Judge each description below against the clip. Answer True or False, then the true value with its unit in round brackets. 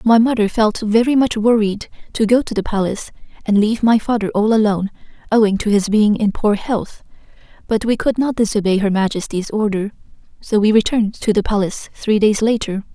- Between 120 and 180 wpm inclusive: False (190 wpm)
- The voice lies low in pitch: False (215 Hz)